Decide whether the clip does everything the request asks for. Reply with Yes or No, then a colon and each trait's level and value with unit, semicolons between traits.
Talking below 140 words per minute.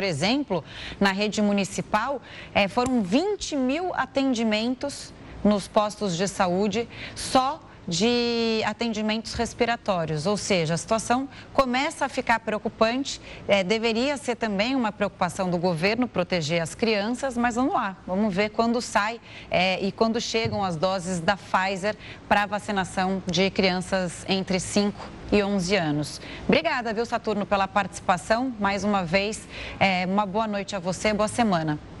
No: average, 145 wpm